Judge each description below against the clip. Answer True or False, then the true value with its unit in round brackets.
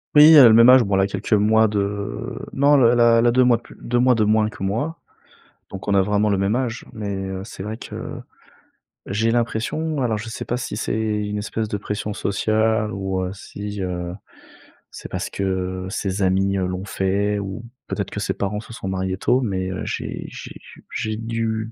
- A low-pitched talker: True (105 Hz)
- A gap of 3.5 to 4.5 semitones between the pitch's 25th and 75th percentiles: False (2.9 semitones)